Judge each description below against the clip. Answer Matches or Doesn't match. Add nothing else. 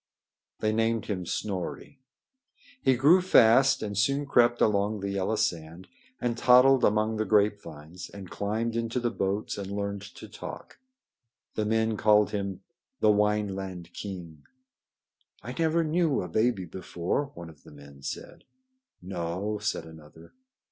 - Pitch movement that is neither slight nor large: Matches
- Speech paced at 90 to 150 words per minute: Matches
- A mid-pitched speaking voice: Doesn't match